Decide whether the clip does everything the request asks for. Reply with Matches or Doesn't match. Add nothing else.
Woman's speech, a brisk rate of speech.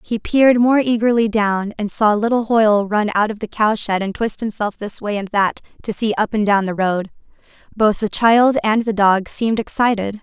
Matches